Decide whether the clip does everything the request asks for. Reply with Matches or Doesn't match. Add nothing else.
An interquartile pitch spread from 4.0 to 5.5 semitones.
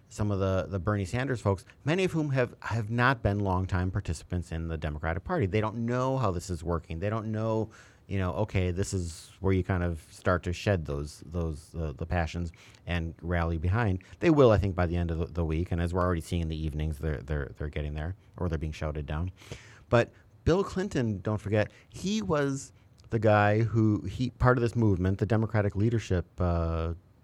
Matches